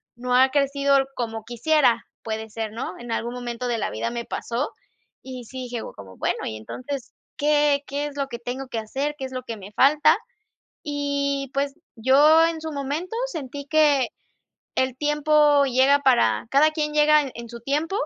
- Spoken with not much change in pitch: No, average, 3.6 semitones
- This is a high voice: Yes, very high, 275 Hz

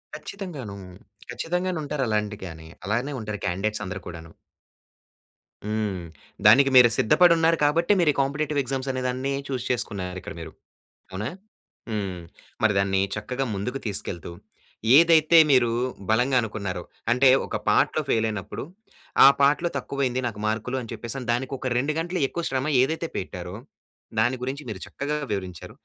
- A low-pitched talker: Yes, low, 125 Hz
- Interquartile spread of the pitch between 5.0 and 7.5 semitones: Yes, average, 5.3 semitones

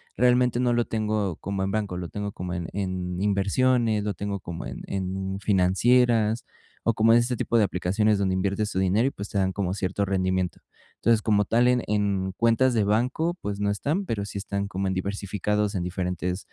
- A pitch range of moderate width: Yes, average, 3.0 semitones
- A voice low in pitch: Yes, low, 100 Hz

